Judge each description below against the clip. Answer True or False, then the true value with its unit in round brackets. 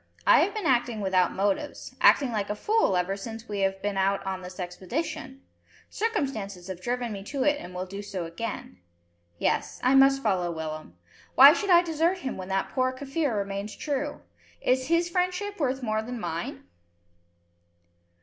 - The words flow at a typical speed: True (175 wpm)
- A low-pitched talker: False (220 Hz)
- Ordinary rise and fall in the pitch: False (6.5 semitones)